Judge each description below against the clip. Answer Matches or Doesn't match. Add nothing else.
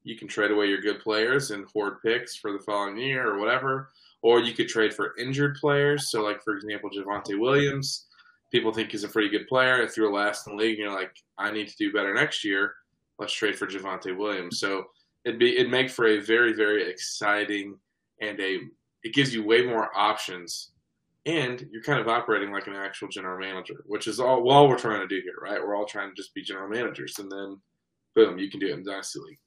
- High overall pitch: Doesn't match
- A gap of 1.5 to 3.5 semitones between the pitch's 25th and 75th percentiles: Doesn't match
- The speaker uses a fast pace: Matches